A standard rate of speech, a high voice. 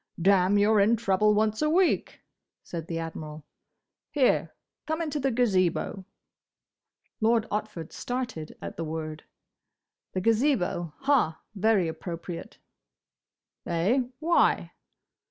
No: slow, 105 wpm; high, 205 Hz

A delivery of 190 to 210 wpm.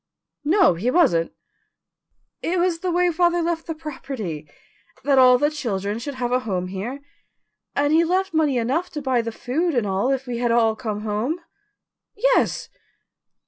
No: average, 170 wpm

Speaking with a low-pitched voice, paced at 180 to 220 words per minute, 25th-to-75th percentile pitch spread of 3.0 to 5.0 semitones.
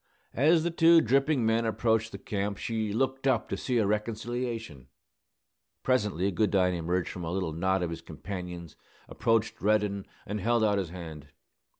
No: low, 105 Hz; average, 165 wpm; average, 4.3 semitones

